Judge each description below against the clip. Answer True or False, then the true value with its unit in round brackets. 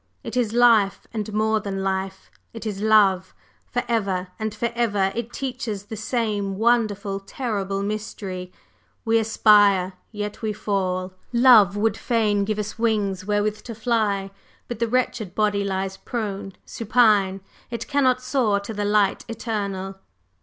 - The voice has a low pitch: False (210 Hz)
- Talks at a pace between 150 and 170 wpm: False (140 wpm)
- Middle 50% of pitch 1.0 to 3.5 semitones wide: True (2.6 semitones)